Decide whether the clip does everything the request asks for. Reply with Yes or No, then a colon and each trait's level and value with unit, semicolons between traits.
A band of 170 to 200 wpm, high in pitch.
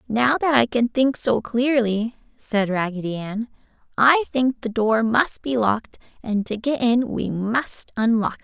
Yes: average, 180 wpm; high, 235 Hz